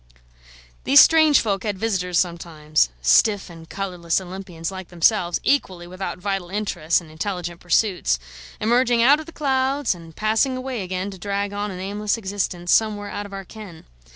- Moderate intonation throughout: Yes, average, 3.6 semitones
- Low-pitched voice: No, high, 195 Hz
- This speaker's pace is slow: No, average, 165 wpm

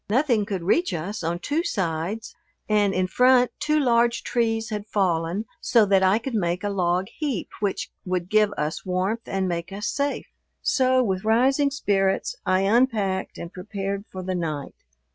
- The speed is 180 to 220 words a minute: No, average, 170 wpm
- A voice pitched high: Yes, high, 200 Hz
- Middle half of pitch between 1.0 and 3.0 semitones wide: No, average, 4.1 semitones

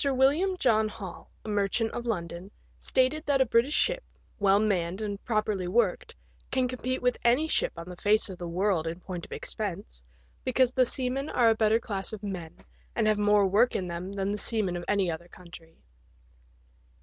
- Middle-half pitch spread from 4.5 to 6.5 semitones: Yes, average, 5.1 semitones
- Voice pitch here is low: No, high, 210 Hz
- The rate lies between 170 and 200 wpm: Yes, average, 190 wpm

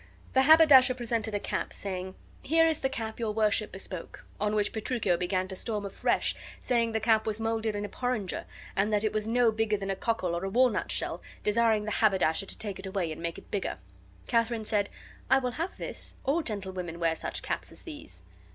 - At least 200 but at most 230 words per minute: Yes, fast, 205 wpm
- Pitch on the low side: No, high, 215 Hz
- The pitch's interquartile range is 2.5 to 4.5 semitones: Yes, average, 3.2 semitones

